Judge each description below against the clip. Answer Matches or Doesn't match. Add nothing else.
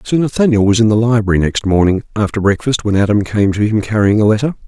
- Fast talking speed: Matches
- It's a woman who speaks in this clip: Doesn't match